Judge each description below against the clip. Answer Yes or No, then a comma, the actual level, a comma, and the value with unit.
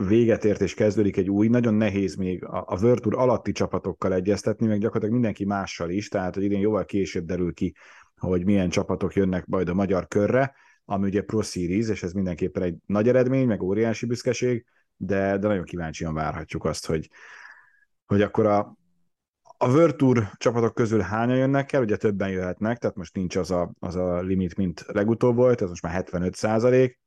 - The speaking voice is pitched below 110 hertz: Yes, low, 100 Hz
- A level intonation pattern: No, average, 3.5 semitones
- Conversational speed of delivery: No, fast, 190 wpm